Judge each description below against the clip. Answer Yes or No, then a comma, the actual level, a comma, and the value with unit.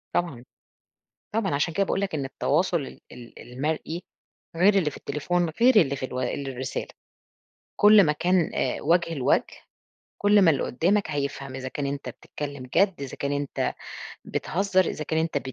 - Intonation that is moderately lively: Yes, average, 4.7 semitones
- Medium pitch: Yes, medium, 155 Hz